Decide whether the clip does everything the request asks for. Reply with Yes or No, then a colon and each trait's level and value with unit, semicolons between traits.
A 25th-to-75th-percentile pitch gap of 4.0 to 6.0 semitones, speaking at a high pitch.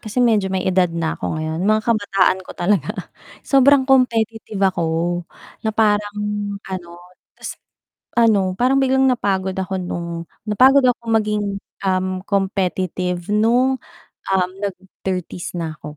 No: average, 3.5 semitones; high, 200 Hz